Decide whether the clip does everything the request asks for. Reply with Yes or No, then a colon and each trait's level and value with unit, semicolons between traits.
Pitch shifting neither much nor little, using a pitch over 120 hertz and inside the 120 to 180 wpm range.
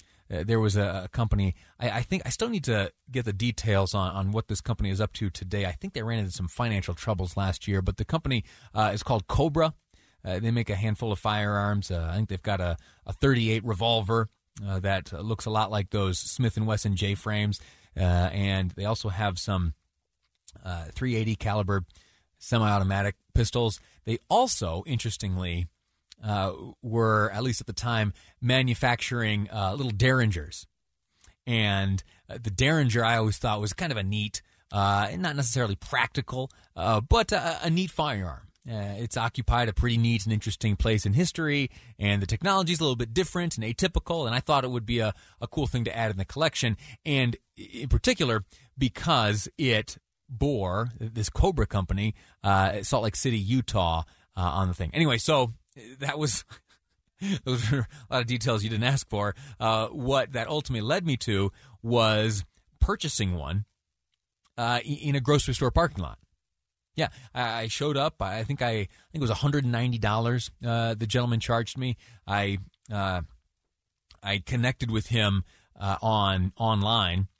No: average, 3.9 semitones; low, 110 Hz; average, 175 wpm